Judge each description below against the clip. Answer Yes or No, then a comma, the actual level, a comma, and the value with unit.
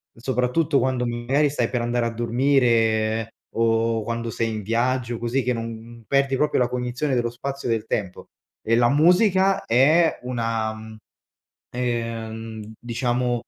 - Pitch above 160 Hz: No, low, 120 Hz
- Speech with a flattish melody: Yes, narrow, 2.2 semitones